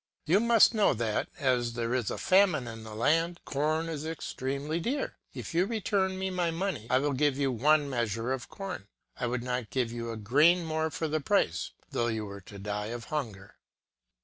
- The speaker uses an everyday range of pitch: No, wide, 6.0 semitones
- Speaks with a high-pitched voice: No, medium, 140 Hz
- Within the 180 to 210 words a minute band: Yes, average, 200 wpm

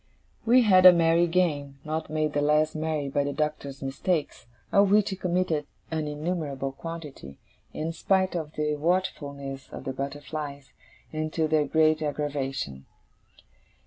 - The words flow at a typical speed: Yes, average, 145 wpm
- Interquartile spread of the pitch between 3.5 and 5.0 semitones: No, average, 2.8 semitones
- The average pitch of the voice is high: No, medium, 155 Hz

